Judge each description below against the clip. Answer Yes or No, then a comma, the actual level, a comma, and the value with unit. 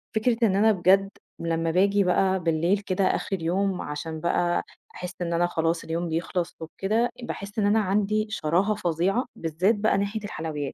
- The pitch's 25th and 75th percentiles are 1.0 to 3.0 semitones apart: No, average, 3.4 semitones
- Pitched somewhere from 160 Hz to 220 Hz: Yes, medium, 185 Hz